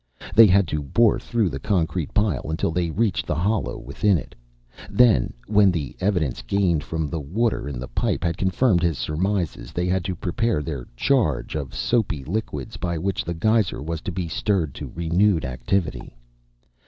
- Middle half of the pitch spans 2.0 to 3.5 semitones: No, average, 4.9 semitones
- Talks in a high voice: No, very low, 90 Hz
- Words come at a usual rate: Yes, average, 180 wpm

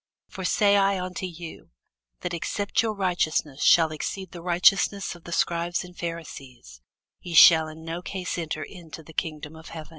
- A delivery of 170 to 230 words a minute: Yes, average, 175 wpm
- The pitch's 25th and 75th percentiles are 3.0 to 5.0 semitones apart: No, narrow, 2.4 semitones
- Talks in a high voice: No, medium, 170 Hz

